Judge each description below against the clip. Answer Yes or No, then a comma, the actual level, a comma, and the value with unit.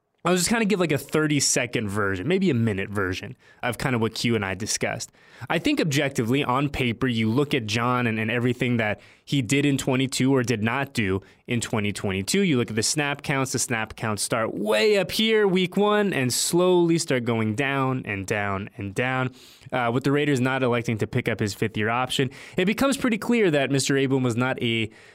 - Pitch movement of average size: Yes, average, 4.4 semitones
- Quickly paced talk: Yes, fast, 215 wpm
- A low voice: Yes, low, 130 Hz